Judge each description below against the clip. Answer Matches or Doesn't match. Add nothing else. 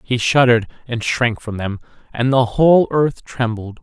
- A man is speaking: Matches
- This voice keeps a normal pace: Matches